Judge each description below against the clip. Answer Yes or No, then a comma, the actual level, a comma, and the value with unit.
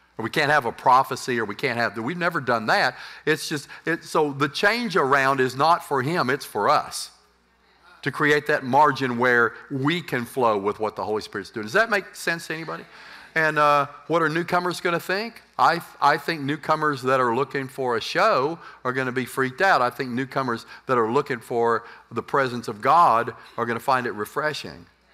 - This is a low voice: No, medium, 145 Hz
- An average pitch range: Yes, average, 3.8 semitones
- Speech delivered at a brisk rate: Yes, fast, 210 wpm